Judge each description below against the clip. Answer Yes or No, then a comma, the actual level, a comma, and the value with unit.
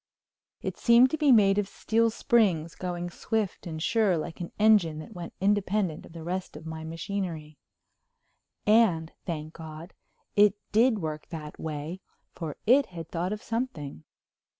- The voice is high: No, medium, 180 Hz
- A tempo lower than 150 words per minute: No, average, 155 wpm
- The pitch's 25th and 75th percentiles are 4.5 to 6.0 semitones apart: Yes, average, 4.9 semitones